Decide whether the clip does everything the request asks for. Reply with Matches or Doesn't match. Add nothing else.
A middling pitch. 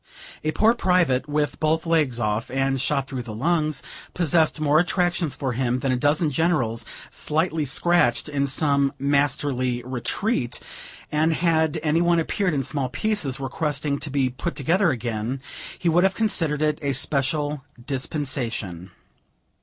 Matches